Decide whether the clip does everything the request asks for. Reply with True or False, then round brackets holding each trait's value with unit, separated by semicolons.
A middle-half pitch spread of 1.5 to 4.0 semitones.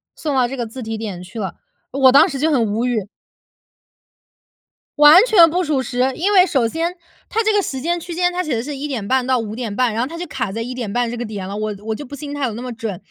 False (5.1 semitones)